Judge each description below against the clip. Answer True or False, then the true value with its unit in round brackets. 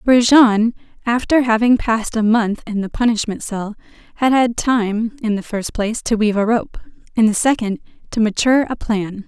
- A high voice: True (225 Hz)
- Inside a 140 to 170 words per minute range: False (180 wpm)